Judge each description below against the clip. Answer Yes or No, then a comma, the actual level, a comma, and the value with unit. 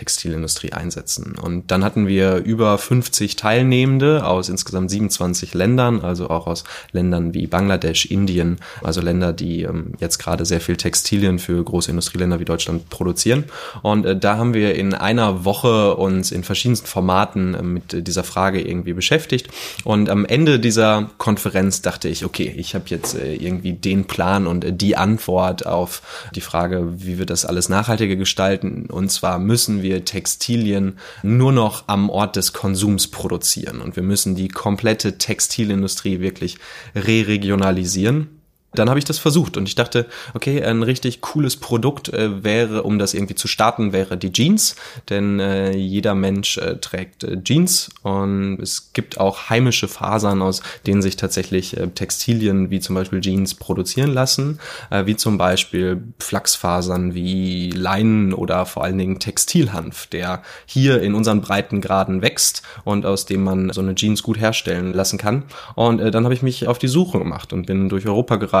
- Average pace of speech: Yes, average, 165 wpm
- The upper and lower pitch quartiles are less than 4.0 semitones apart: Yes, average, 3.3 semitones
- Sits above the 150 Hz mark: No, low, 100 Hz